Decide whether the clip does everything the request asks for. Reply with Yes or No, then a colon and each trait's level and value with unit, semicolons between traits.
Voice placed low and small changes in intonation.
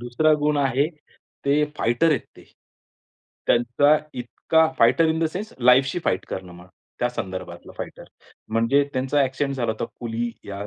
No: low, 125 Hz; average, 4.3 semitones